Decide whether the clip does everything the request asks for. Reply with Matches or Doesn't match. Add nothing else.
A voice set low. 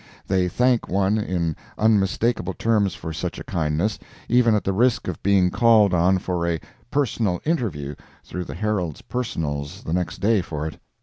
Matches